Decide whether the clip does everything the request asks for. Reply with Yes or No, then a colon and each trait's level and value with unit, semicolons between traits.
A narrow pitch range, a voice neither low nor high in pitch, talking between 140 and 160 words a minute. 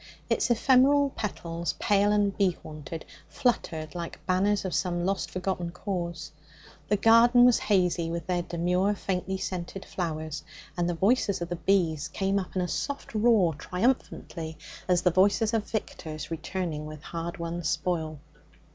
No: average, 3.3 semitones; medium, 180 Hz; average, 150 wpm